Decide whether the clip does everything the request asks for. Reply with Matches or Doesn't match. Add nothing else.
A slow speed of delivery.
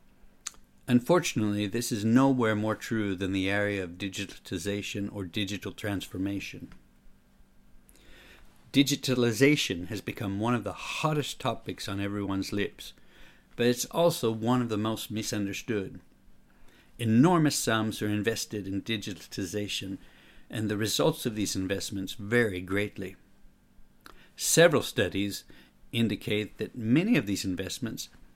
Matches